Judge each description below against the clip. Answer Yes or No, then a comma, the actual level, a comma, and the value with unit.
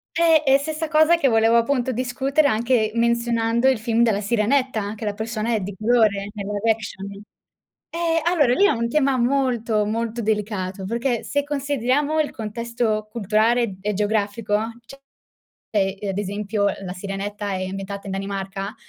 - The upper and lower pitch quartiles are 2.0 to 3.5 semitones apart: No, average, 3.9 semitones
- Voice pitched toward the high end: Yes, high, 225 Hz